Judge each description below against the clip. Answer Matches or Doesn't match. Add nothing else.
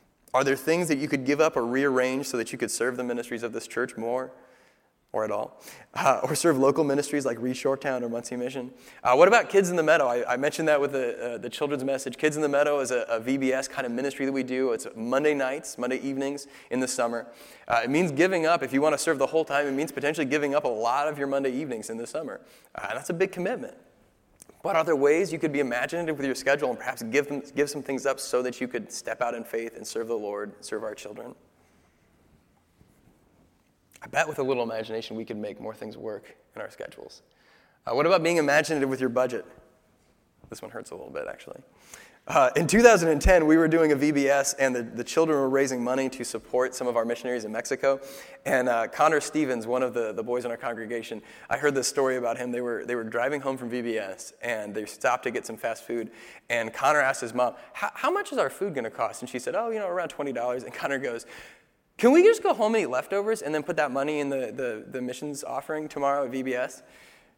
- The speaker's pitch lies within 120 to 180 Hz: Matches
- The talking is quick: Matches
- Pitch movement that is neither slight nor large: Matches